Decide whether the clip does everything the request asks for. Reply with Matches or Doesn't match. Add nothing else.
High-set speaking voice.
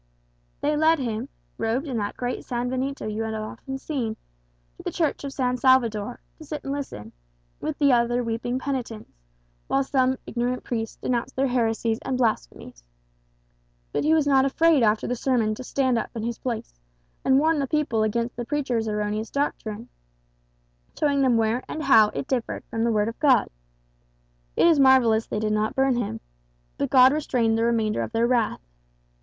Matches